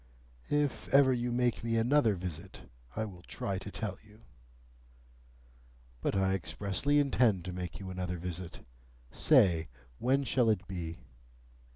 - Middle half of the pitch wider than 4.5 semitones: Yes, average, 5.2 semitones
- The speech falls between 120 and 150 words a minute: Yes, average, 140 wpm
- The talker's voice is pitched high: No, low, 100 Hz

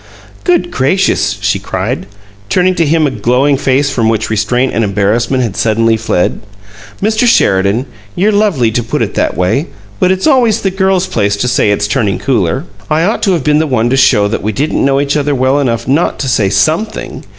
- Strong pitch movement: Yes, wide, 6.9 semitones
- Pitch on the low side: Yes, low, 130 Hz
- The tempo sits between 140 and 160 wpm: No, fast, 205 wpm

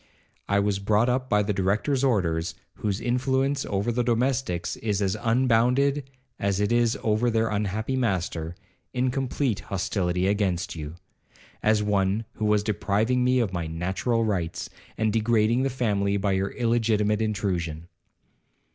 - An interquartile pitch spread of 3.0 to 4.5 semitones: Yes, average, 3.6 semitones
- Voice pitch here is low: Yes, low, 105 Hz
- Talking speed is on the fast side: No, average, 145 wpm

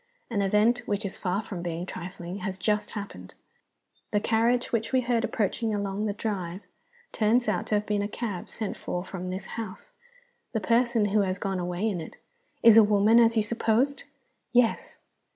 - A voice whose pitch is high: Yes, high, 210 Hz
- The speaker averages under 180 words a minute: No, average, 190 wpm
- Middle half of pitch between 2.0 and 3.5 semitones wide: Yes, average, 2.9 semitones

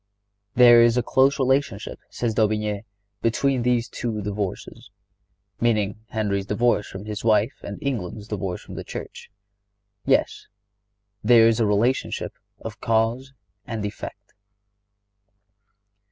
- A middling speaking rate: No, slow, 120 wpm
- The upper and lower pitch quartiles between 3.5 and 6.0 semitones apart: No, narrow, 2.6 semitones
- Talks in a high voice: No, low, 110 Hz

